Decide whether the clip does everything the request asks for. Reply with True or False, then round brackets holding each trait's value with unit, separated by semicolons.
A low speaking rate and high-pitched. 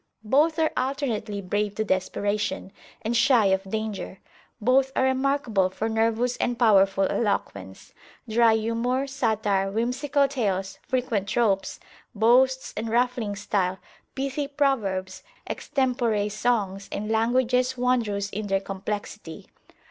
True (120 wpm; 220 Hz)